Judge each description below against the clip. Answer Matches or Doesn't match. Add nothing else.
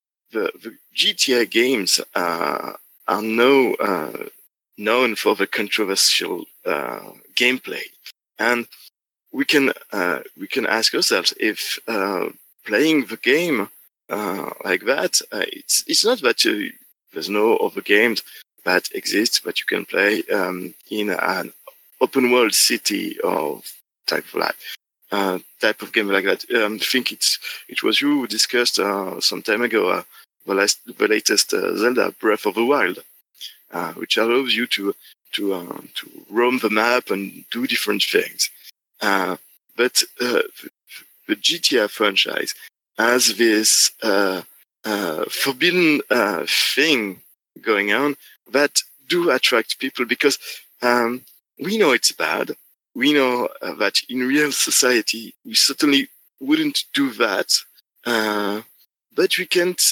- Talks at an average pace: Matches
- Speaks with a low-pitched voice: Doesn't match